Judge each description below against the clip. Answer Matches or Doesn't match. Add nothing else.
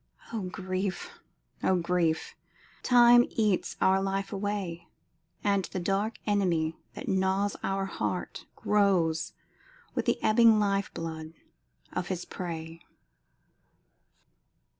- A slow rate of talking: Matches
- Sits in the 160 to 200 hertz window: Matches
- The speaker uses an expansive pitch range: Doesn't match